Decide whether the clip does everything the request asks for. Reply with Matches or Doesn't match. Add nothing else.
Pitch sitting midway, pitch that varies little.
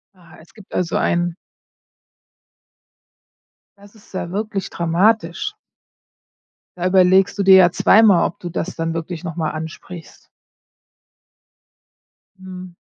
Matches